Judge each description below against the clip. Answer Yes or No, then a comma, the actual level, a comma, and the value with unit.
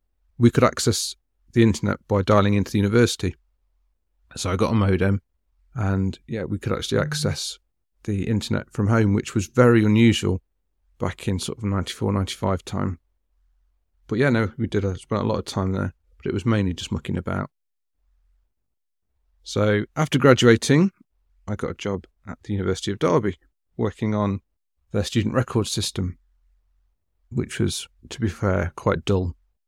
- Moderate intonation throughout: Yes, average, 3.8 semitones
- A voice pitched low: Yes, low, 100 Hz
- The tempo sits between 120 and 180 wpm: Yes, average, 160 wpm